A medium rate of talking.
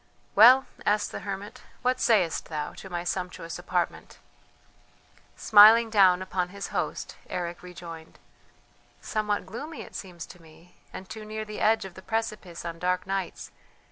Yes: average, 150 wpm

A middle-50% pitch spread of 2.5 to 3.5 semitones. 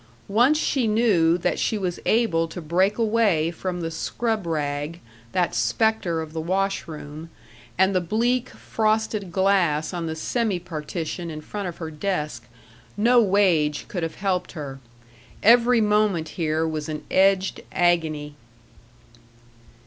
No: average, 4.8 semitones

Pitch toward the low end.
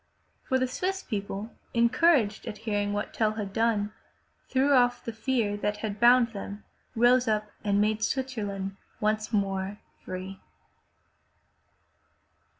No: high, 215 Hz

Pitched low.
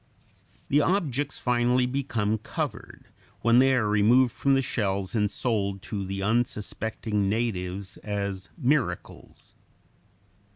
Yes: low, 110 Hz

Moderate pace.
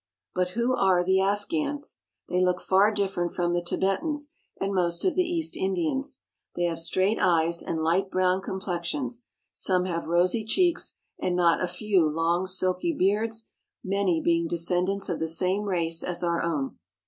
Yes: average, 165 wpm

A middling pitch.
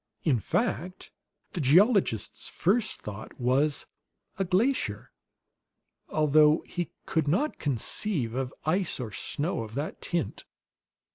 Yes: medium, 155 Hz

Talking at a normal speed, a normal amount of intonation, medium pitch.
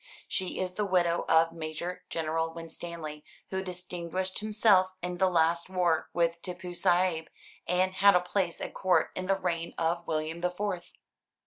No: average, 160 wpm; narrow, 2.0 semitones; medium, 175 Hz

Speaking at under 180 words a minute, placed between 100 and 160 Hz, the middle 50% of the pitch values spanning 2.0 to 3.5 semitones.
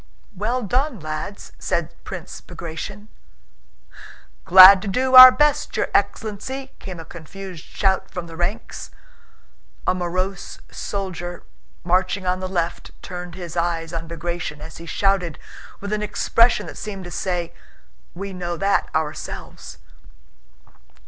No: slow, 135 wpm; medium, 185 Hz; average, 2.8 semitones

